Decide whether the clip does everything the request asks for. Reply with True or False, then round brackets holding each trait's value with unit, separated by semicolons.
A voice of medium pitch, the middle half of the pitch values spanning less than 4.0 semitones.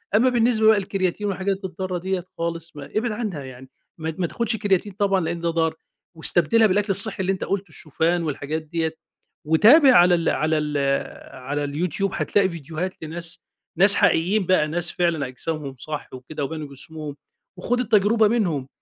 False (175 Hz; 4.3 semitones)